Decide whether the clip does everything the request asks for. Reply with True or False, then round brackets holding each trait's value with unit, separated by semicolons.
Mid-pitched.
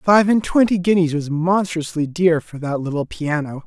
True (165 Hz)